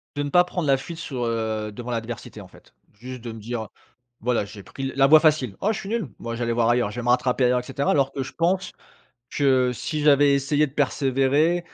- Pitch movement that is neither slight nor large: Yes, average, 3.6 semitones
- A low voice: Yes, low, 130 Hz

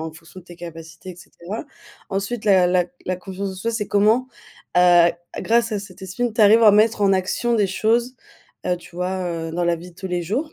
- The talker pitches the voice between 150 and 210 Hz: Yes, high, 190 Hz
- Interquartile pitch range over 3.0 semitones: Yes, average, 3.6 semitones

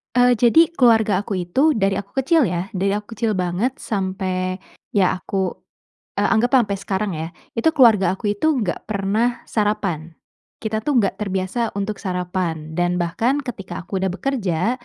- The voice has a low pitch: No, high, 200 Hz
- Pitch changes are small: No, average, 4.0 semitones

